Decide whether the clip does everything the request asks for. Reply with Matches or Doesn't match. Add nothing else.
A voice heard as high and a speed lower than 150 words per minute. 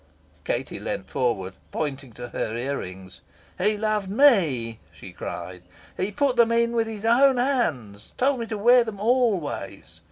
Doesn't match